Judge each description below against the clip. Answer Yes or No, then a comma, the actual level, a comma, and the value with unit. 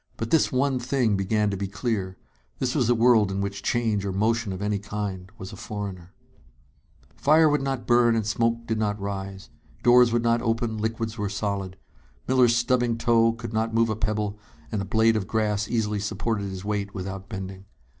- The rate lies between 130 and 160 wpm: No, average, 195 wpm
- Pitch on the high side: No, low, 110 Hz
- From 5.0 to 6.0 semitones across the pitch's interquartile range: No, average, 2.8 semitones